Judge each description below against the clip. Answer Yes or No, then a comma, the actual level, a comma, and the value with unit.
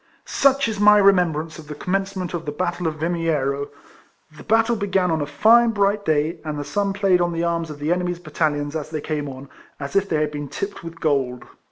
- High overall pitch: No, medium, 165 Hz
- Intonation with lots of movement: No, average, 4.7 semitones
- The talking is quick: Yes, fast, 225 wpm